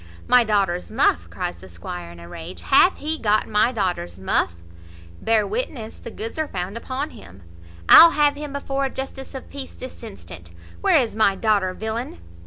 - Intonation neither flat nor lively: No, wide, 7.6 semitones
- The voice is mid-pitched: No, high, 220 Hz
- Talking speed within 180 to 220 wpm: Yes, average, 185 wpm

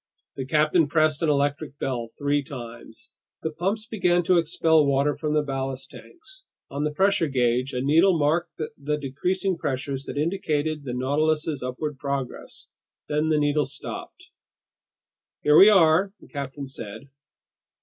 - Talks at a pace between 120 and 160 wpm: Yes, average, 150 wpm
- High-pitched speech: No, medium, 150 Hz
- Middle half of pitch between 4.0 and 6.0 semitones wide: No, average, 3.1 semitones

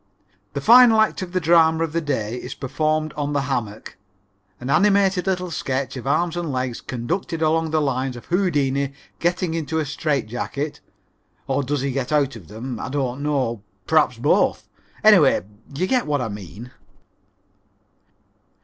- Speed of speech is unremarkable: Yes, average, 165 wpm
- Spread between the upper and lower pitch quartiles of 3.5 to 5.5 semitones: Yes, average, 4.3 semitones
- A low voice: No, medium, 145 Hz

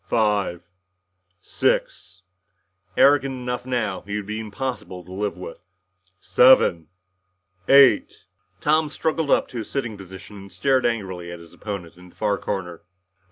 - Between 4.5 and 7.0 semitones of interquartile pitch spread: Yes, average, 5.2 semitones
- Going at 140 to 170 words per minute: Yes, average, 150 wpm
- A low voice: Yes, low, 105 Hz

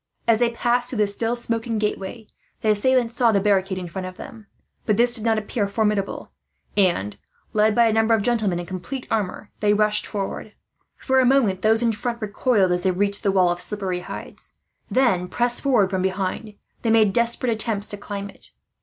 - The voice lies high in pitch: Yes, high, 210 Hz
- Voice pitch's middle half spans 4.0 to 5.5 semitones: No, average, 3.1 semitones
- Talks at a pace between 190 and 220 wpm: Yes, average, 200 wpm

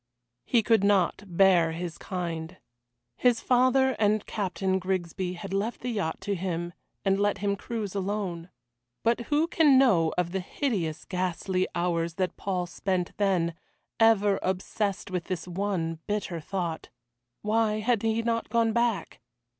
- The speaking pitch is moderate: No, high, 195 Hz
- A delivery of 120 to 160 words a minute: Yes, average, 145 wpm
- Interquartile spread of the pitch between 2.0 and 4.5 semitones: Yes, average, 3.8 semitones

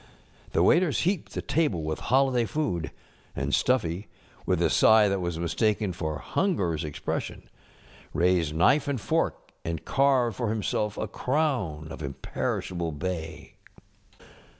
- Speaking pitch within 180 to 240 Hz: No, very low, 95 Hz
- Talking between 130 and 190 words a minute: Yes, average, 140 wpm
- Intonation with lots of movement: Yes, wide, 8.0 semitones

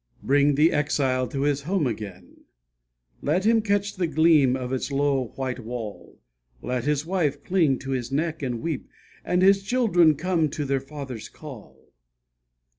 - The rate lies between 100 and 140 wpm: No, average, 160 wpm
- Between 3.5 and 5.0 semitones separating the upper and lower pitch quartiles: Yes, average, 4.3 semitones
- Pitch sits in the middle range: Yes, medium, 145 Hz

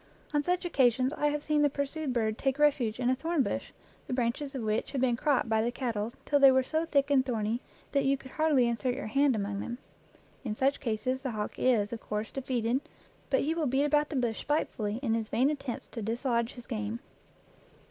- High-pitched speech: Yes, very high, 255 Hz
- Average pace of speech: No, fast, 220 wpm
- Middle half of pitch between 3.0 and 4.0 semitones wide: Yes, average, 3.7 semitones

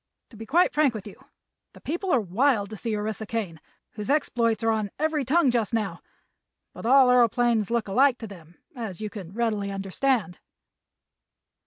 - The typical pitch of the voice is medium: No, high, 225 Hz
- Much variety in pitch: No, average, 3.7 semitones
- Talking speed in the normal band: Yes, average, 175 wpm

